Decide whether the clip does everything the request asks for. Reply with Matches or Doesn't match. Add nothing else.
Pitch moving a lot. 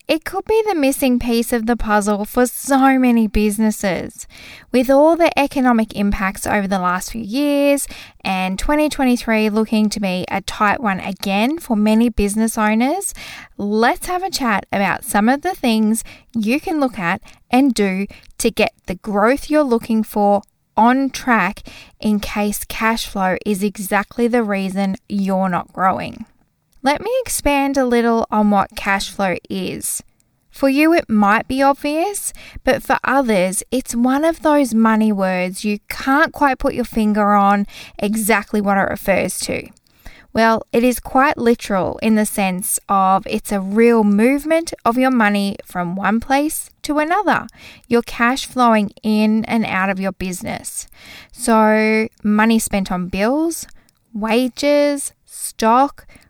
Doesn't match